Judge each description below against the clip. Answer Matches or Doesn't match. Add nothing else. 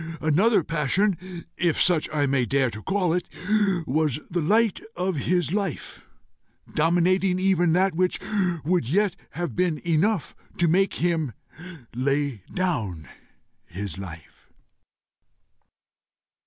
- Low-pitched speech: Doesn't match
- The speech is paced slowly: Matches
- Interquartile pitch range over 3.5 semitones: Matches